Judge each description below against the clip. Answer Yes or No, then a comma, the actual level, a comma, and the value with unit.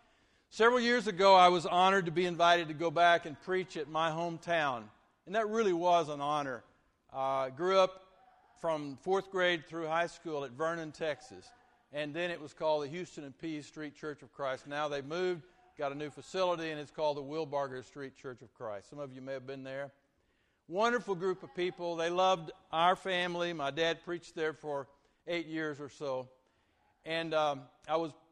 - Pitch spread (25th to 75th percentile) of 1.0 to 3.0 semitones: No, average, 3.8 semitones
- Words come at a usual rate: Yes, average, 195 wpm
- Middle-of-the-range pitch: Yes, medium, 160 Hz